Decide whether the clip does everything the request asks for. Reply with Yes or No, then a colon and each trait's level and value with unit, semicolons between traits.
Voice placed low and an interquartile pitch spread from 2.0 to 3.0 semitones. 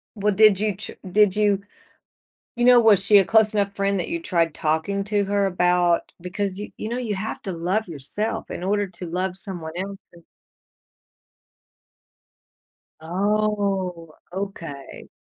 No: high, 195 Hz; average, 2.7 semitones